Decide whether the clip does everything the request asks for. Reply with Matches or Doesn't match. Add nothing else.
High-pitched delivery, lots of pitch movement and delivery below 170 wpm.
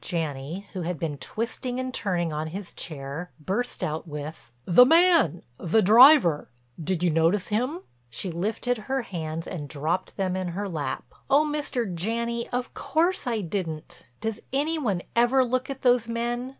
Matches